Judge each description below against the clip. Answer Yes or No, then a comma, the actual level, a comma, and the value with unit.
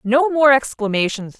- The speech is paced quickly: No, slow, 130 wpm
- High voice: Yes, very high, 250 Hz